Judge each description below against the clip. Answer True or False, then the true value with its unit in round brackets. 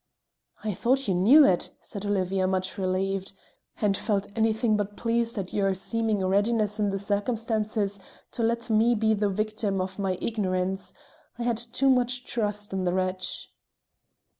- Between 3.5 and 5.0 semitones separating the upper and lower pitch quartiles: False (3.0 semitones)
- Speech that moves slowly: False (160 wpm)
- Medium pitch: False (205 Hz)